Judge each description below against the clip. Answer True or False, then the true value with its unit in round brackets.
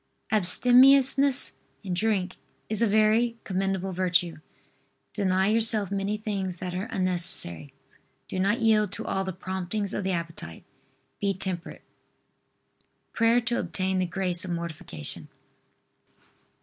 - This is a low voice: False (190 Hz)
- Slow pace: True (125 wpm)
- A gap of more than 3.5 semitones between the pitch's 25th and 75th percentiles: False (3.1 semitones)